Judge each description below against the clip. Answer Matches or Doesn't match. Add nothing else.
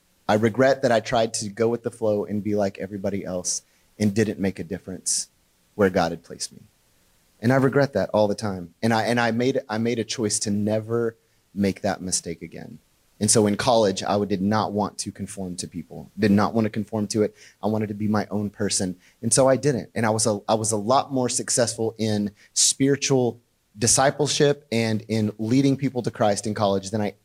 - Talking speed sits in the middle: Doesn't match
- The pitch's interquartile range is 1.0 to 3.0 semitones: Matches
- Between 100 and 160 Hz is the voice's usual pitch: Matches